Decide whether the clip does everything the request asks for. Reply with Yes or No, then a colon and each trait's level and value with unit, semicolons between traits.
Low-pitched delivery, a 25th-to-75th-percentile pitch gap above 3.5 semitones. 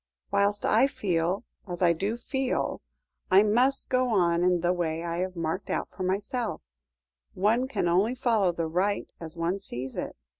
No: high, 190 Hz; average, 4.2 semitones